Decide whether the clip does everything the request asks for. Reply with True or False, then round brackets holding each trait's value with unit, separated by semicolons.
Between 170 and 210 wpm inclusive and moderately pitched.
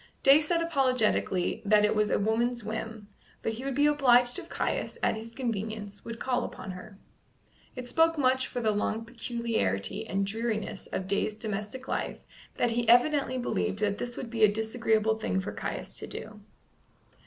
False (175 wpm; 225 Hz)